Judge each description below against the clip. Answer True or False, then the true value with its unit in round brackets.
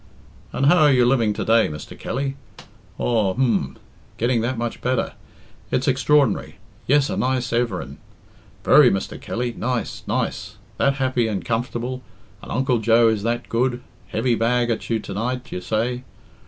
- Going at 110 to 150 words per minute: False (160 wpm)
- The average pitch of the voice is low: True (120 Hz)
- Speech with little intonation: True (2.2 semitones)